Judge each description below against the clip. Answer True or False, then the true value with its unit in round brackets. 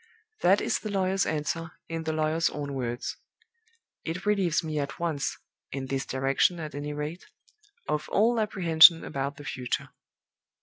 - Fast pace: False (155 wpm)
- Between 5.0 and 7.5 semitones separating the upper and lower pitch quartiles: False (3.6 semitones)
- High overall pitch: False (155 Hz)